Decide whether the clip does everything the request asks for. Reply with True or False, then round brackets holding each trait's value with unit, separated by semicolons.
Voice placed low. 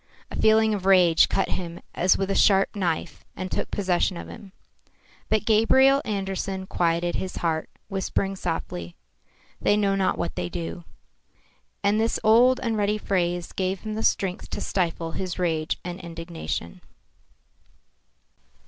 False (190 Hz)